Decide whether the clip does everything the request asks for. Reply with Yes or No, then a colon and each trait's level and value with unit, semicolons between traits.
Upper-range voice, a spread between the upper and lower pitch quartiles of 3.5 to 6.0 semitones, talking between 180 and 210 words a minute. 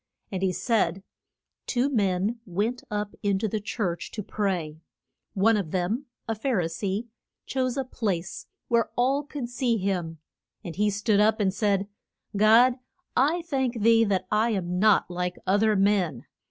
No: high, 210 Hz; average, 3.8 semitones; average, 165 wpm